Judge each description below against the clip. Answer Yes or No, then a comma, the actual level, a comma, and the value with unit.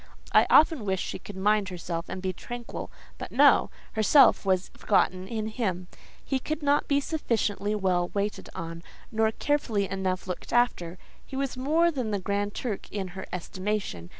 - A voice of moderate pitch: No, high, 205 Hz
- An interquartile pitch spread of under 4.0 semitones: No, average, 4.6 semitones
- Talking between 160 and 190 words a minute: Yes, average, 165 wpm